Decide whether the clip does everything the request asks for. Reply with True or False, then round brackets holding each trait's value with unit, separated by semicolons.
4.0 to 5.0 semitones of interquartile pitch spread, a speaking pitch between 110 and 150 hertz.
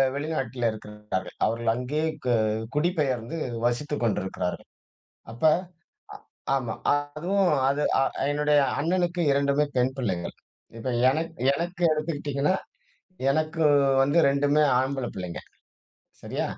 True (4.3 semitones; 140 Hz)